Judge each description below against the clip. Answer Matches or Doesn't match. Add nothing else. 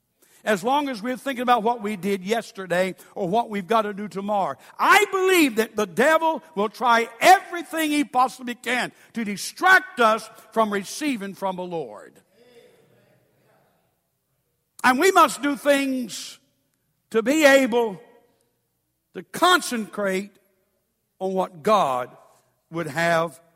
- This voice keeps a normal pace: Doesn't match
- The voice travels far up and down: Matches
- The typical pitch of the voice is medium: Doesn't match